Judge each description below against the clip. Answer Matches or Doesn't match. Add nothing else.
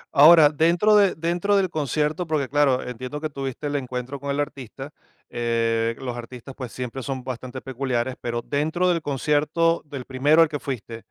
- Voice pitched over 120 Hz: Matches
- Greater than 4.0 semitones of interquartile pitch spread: Doesn't match